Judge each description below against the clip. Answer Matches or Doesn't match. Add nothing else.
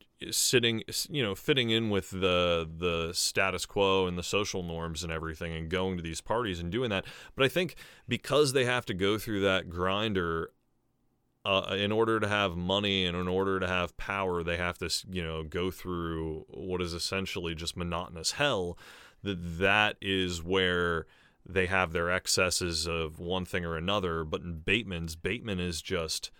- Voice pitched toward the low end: Matches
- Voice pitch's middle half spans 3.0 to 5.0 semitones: Doesn't match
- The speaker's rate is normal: Matches